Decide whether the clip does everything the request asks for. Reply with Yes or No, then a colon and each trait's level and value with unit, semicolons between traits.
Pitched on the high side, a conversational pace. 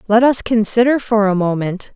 Yes: high, 215 Hz; average, 185 wpm